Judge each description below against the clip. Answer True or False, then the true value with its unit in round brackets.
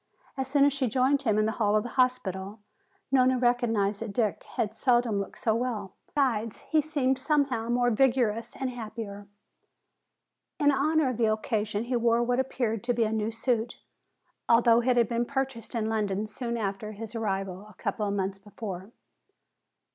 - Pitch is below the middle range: False (230 Hz)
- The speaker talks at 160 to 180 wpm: True (175 wpm)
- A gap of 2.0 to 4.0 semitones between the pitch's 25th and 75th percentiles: True (3.1 semitones)